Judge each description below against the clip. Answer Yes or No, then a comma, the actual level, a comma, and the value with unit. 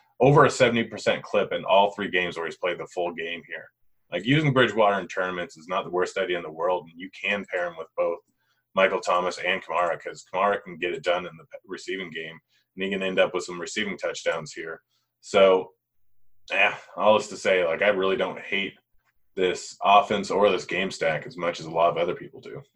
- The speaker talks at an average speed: No, fast, 225 wpm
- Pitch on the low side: Yes, low, 100 Hz